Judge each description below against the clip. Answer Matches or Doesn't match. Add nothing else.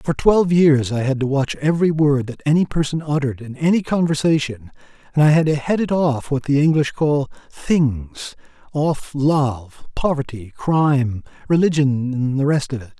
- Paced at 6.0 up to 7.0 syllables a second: Doesn't match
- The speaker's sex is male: Matches